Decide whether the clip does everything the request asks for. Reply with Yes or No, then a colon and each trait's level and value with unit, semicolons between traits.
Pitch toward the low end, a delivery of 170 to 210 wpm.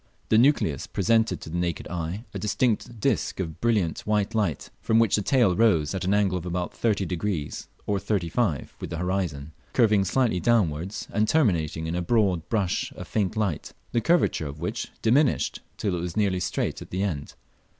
Yes: very low, 95 Hz; average, 185 wpm